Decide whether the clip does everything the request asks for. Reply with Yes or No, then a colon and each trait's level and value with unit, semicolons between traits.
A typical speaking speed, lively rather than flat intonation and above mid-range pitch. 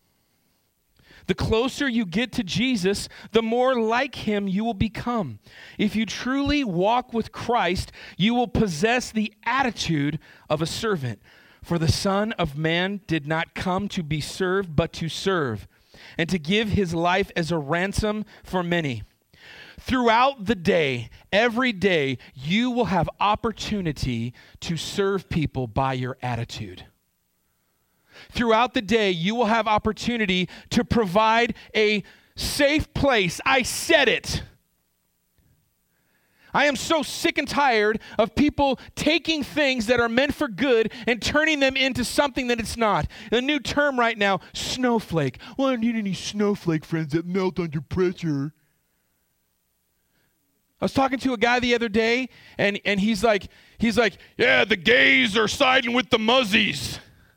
Yes: average, 150 wpm; wide, 6.3 semitones; high, 210 Hz